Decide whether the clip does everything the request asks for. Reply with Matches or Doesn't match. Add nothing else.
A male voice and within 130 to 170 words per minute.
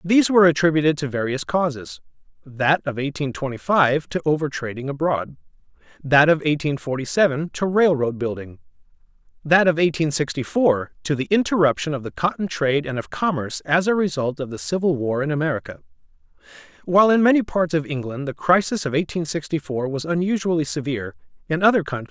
Doesn't match